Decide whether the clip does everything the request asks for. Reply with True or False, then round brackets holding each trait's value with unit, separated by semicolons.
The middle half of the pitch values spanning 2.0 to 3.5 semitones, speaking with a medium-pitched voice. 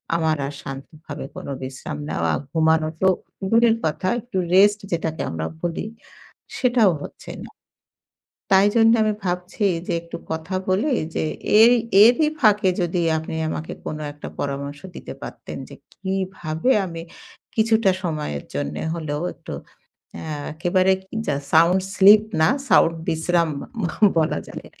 False (4.3 semitones; 170 Hz)